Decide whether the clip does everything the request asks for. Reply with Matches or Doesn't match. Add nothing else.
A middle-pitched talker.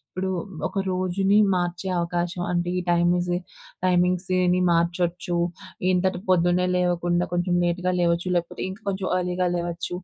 Matches